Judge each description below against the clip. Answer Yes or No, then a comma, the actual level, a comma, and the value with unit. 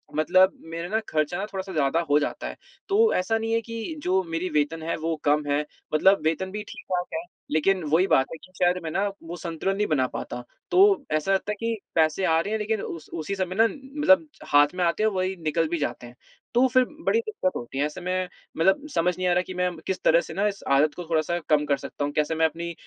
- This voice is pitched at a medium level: Yes, medium, 180 Hz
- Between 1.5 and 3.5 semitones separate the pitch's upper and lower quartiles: No, average, 4.5 semitones